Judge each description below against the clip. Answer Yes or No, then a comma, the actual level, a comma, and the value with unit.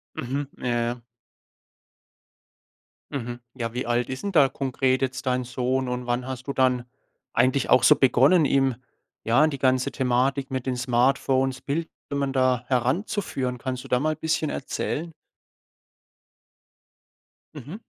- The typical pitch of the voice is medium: No, low, 130 Hz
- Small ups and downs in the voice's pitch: Yes, narrow, 1.8 semitones